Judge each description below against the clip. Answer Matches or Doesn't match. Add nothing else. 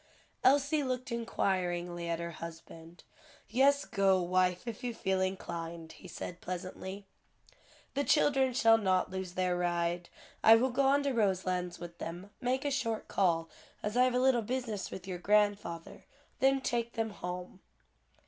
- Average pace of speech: Matches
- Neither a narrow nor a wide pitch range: Doesn't match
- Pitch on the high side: Matches